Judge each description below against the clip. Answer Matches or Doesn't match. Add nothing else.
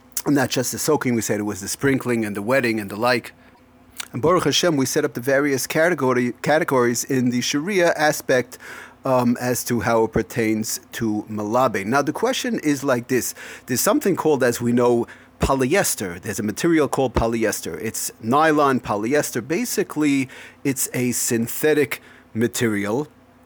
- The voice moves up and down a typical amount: Matches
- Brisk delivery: Doesn't match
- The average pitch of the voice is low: Matches